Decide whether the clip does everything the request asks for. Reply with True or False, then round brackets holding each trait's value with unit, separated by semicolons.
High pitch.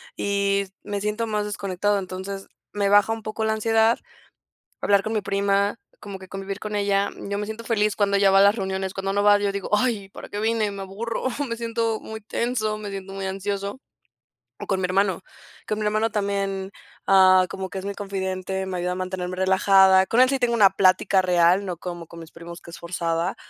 True (200 Hz)